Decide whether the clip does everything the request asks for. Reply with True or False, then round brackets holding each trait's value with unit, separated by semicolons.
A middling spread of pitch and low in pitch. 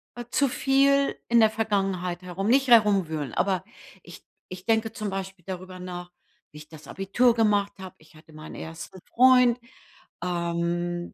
False (4.5 semitones; 190 Hz)